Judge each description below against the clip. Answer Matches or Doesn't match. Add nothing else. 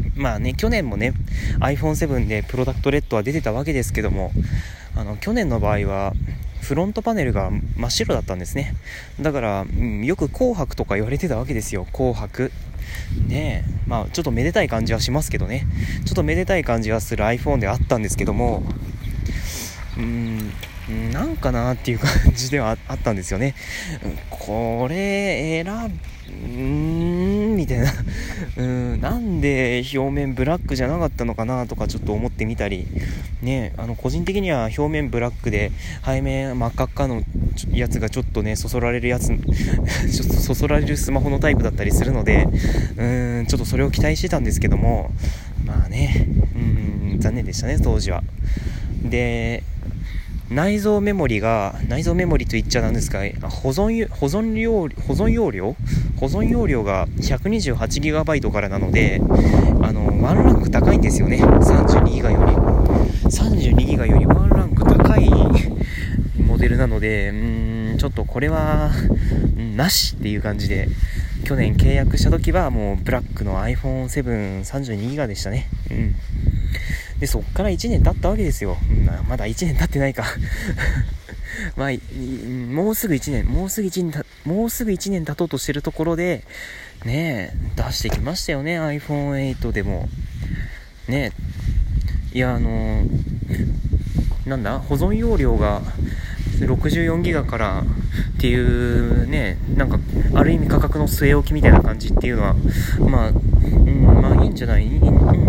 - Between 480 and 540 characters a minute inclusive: Doesn't match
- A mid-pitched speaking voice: Doesn't match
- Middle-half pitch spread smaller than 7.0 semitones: Matches